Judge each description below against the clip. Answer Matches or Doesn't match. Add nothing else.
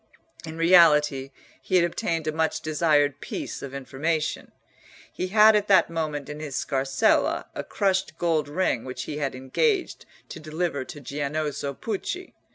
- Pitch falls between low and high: Matches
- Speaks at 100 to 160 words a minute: Matches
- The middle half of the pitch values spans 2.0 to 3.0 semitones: Doesn't match